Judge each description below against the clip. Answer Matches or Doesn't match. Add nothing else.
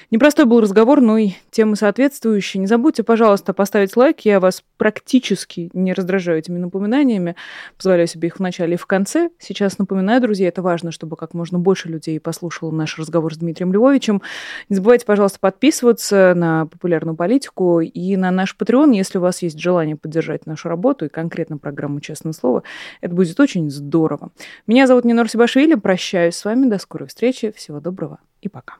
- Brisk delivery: Matches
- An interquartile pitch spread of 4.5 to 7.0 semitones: Matches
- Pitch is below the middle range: Doesn't match